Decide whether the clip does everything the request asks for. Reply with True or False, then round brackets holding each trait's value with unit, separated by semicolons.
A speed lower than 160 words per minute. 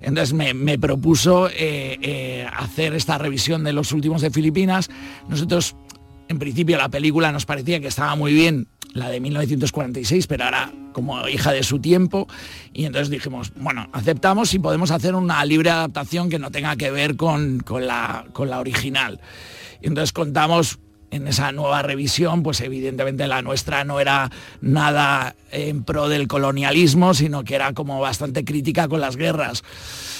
False (165 wpm)